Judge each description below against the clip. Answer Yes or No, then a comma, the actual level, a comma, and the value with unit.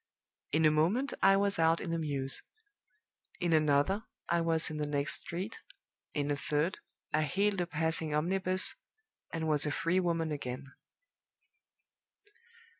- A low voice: No, medium, 160 Hz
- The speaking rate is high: No, average, 145 wpm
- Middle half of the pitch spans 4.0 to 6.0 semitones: No, average, 3.1 semitones